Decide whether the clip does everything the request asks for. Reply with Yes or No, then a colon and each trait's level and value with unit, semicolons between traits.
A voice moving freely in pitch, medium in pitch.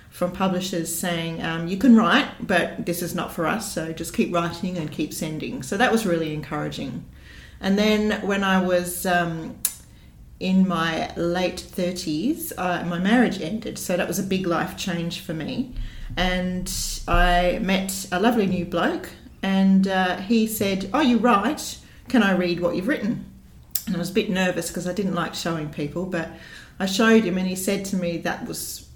No: average, 2.7 semitones; medium, 180 Hz